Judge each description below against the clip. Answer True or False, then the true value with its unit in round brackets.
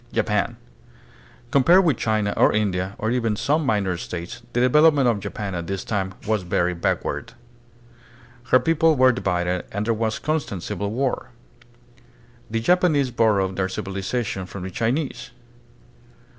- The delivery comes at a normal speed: True (145 wpm)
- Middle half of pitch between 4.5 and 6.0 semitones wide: True (5.1 semitones)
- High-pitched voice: False (110 Hz)